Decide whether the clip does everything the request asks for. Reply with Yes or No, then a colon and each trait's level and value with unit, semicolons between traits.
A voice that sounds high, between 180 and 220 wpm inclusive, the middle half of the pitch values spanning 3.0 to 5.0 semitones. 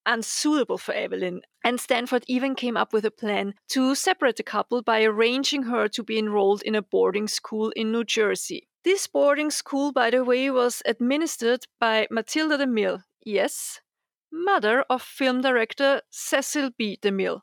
No: high, 245 Hz; average, 160 wpm; average, 4.0 semitones